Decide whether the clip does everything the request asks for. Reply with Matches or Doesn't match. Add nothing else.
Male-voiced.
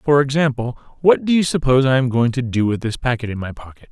Matches